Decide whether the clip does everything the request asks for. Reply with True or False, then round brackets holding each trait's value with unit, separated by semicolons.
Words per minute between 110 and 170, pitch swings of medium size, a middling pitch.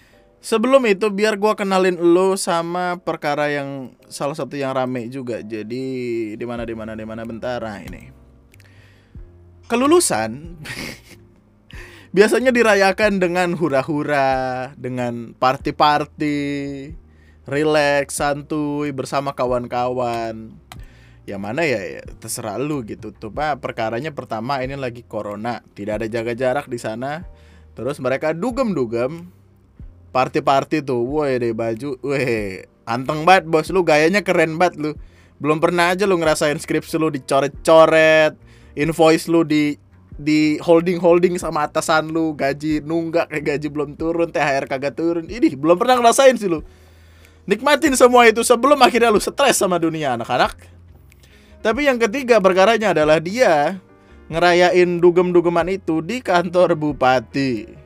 False (125 wpm; 6.4 semitones; 145 Hz)